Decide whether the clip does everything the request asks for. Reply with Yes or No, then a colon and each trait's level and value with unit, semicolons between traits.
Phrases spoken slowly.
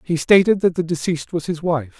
No: fast, 240 wpm